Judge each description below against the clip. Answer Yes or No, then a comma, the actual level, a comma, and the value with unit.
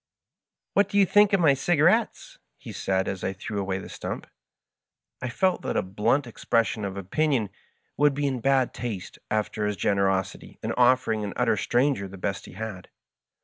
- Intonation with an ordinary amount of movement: No, wide, 6.6 semitones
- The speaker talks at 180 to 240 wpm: Yes, average, 190 wpm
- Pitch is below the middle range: Yes, low, 115 Hz